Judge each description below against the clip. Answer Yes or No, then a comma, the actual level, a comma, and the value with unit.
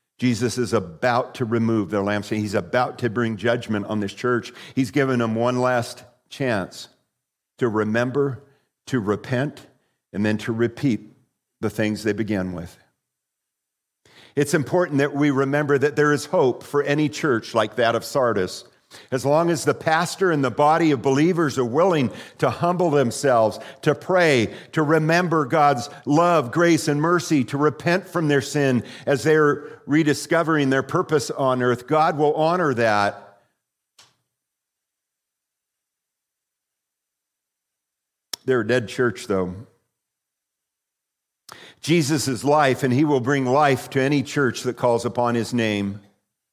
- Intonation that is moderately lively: Yes, average, 4.2 semitones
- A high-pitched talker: No, low, 135 Hz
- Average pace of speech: Yes, average, 145 wpm